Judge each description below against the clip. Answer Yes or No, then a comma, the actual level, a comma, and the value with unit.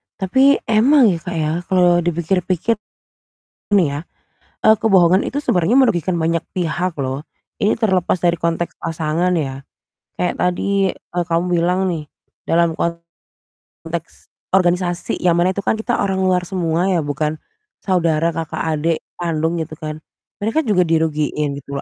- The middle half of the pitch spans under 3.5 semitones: Yes, narrow, 2.6 semitones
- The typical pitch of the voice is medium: Yes, medium, 175 Hz